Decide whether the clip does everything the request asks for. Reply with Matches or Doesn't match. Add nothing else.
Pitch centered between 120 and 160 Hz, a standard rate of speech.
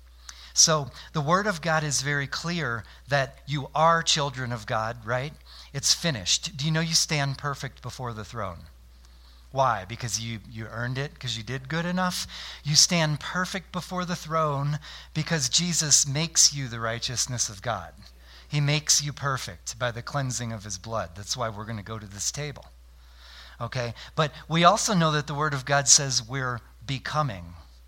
Matches